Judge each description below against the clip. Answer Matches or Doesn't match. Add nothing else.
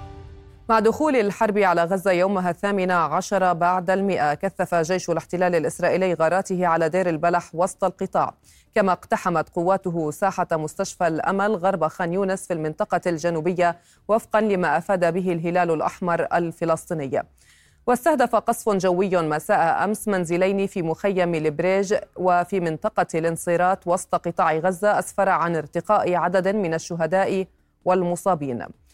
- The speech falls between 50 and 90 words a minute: Doesn't match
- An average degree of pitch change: Doesn't match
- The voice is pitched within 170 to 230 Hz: Matches